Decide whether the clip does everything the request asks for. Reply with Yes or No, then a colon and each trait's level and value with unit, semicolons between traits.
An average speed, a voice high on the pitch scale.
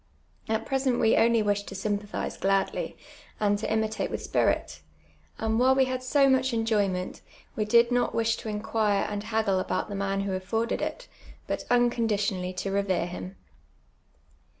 Yes: average, 160 wpm; high, 215 Hz